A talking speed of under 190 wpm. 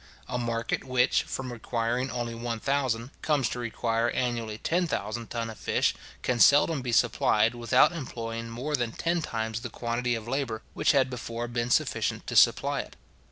Yes: average, 175 wpm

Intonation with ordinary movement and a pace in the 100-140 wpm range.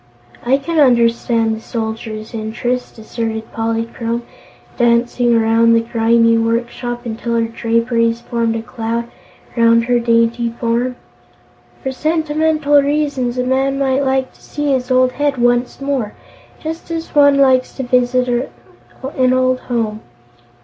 No: narrow, 2.3 semitones; slow, 135 wpm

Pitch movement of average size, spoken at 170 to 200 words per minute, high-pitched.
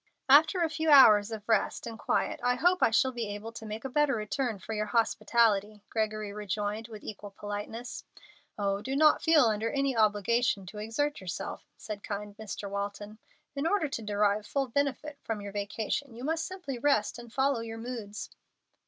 Yes: average, 4.4 semitones; average, 185 wpm; high, 225 Hz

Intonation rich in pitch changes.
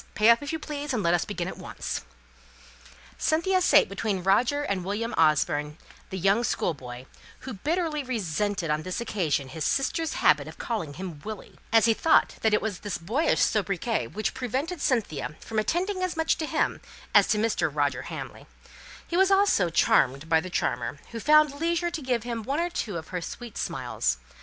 Yes: wide, 8.9 semitones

